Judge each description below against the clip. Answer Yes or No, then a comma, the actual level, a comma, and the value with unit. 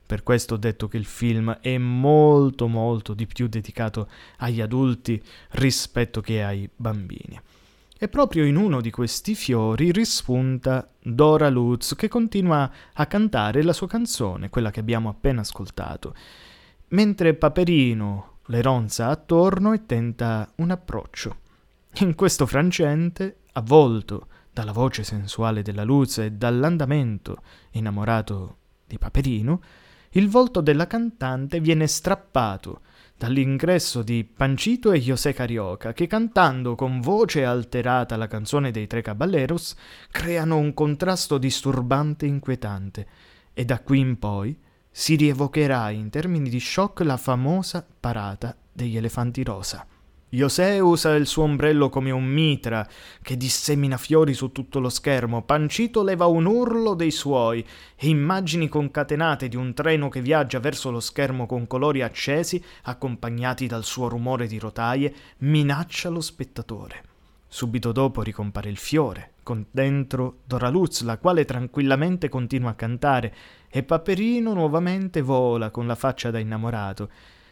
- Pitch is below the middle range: Yes, low, 130 Hz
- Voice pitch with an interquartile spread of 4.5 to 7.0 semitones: Yes, average, 5.3 semitones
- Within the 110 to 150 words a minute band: Yes, average, 135 wpm